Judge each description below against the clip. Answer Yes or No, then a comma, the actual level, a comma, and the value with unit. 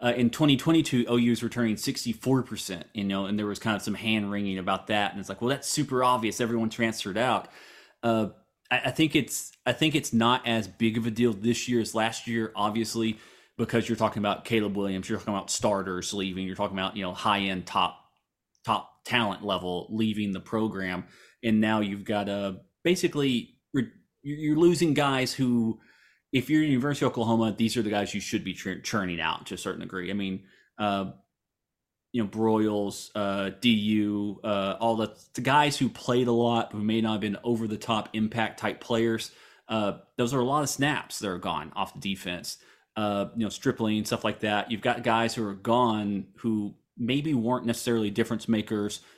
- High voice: No, low, 110 Hz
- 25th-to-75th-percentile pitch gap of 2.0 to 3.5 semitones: Yes, average, 2.8 semitones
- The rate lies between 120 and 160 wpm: No, average, 200 wpm